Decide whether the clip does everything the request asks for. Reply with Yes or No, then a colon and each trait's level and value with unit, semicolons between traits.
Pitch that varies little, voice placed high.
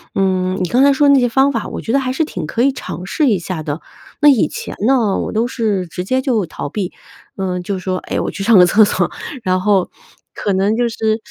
No: average, 5.3 semitones; high, 210 Hz